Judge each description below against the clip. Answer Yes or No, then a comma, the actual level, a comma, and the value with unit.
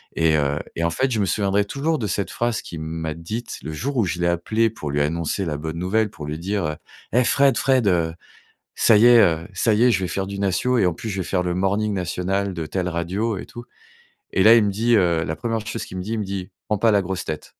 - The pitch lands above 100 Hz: No, very low, 95 Hz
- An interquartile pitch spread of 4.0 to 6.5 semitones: Yes, average, 4.8 semitones